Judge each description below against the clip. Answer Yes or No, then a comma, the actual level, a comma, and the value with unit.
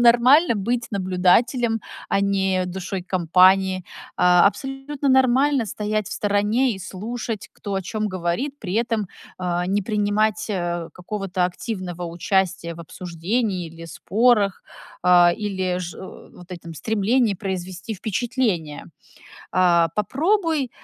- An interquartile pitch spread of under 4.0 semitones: No, average, 4.4 semitones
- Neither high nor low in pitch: No, high, 195 Hz